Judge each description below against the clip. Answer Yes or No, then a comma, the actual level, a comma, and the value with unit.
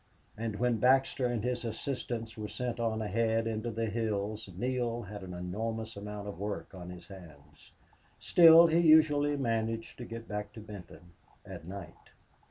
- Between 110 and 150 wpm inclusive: No, average, 165 wpm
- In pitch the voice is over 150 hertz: No, low, 115 Hz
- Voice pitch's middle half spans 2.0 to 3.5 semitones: Yes, average, 3.1 semitones